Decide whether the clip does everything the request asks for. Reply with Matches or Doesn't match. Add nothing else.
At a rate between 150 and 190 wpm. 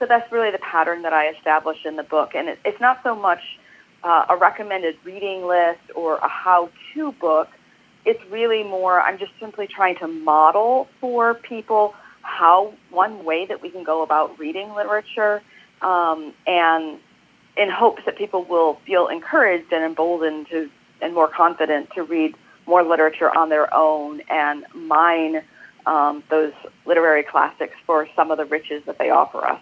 Matches